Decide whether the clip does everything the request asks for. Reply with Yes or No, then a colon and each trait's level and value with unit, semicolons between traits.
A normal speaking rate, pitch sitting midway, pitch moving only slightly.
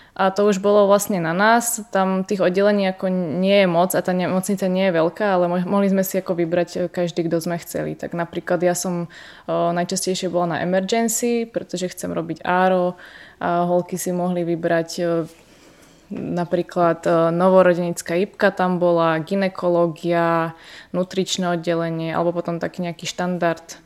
Yes: average, 155 wpm; medium, 180 Hz; narrow, 1.8 semitones